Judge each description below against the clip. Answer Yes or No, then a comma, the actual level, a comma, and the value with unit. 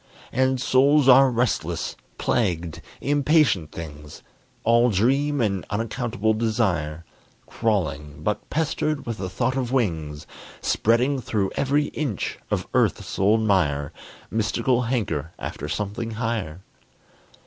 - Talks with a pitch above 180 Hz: No, low, 115 Hz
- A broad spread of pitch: Yes, wide, 6.1 semitones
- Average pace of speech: No, slow, 115 wpm